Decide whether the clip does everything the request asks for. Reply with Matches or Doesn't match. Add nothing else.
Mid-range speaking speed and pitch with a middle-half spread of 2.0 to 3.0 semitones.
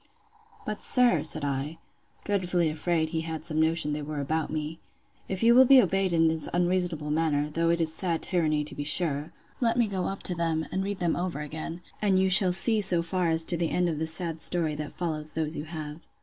Doesn't match